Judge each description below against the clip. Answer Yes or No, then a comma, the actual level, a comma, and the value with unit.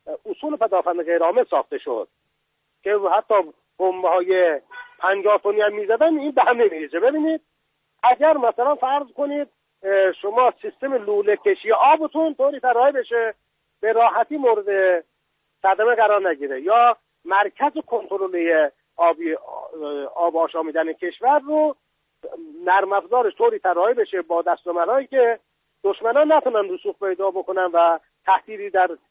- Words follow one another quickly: No, average, 120 wpm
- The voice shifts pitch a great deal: Yes, wide, 7.8 semitones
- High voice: Yes, high, 215 Hz